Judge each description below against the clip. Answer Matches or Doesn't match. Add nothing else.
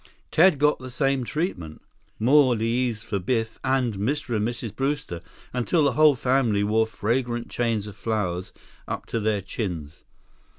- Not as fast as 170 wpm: Matches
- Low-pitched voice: Matches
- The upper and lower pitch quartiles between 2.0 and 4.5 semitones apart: Matches